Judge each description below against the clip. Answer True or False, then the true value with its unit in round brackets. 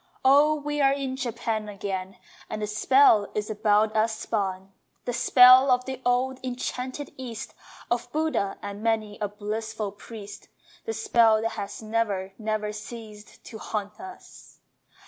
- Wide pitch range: False (3.3 semitones)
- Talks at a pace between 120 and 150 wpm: True (145 wpm)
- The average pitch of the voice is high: True (220 Hz)